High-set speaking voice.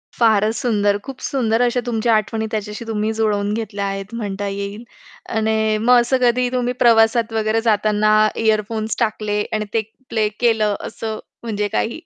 Yes: high, 220 Hz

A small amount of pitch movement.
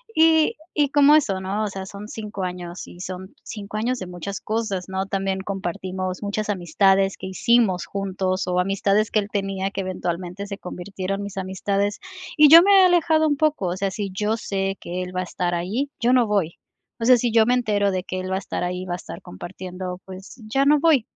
No: average, 3.1 semitones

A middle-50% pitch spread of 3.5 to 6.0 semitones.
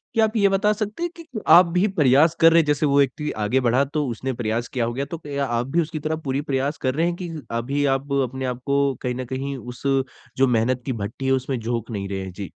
Yes: average, 4.4 semitones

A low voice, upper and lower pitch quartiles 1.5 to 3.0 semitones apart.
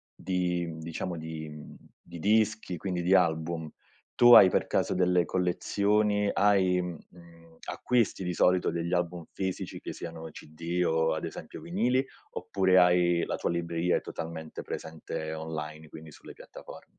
Yes: very low, 85 Hz; narrow, 2.4 semitones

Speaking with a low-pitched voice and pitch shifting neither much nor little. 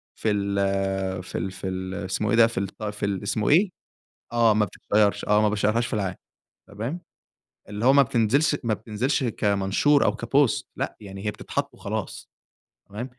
Yes: low, 105 Hz; average, 3.0 semitones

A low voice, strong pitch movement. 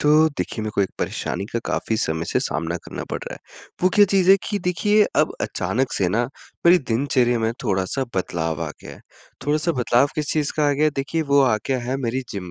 Yes: low, 130 Hz; wide, 6.5 semitones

